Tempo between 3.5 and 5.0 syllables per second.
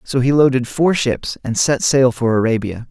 Yes: 4.7 syllables/s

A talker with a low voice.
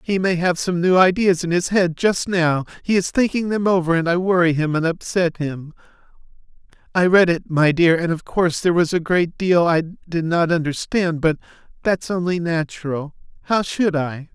No: medium, 170 Hz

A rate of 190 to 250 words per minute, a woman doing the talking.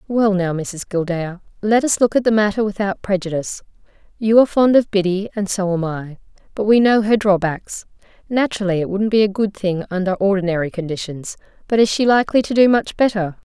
Yes: average, 195 wpm; female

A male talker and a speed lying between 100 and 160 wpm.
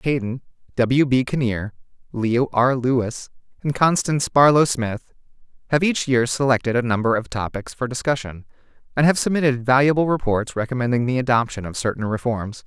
Yes: male; average, 150 wpm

